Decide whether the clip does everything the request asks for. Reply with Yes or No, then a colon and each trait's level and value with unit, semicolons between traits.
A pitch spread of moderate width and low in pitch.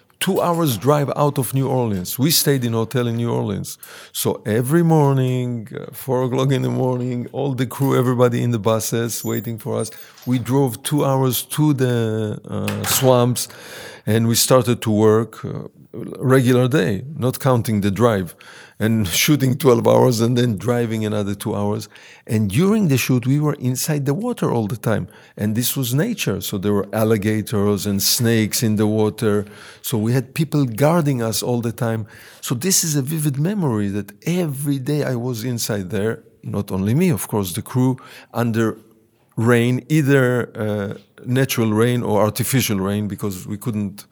Yes: average, 3.6 semitones; low, 120 Hz